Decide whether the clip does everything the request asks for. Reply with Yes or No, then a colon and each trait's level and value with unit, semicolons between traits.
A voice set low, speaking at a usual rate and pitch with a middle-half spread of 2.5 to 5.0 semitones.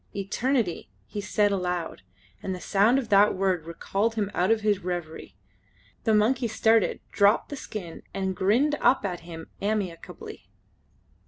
No: high, 200 Hz; average, 150 wpm; average, 3.5 semitones